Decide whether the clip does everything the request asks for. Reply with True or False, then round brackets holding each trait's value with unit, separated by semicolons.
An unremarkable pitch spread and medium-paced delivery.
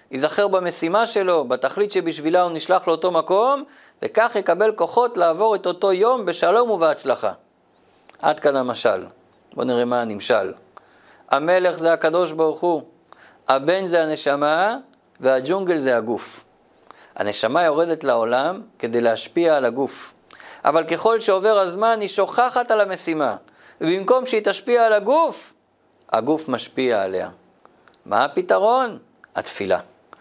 True (4.4 semitones; 125 wpm)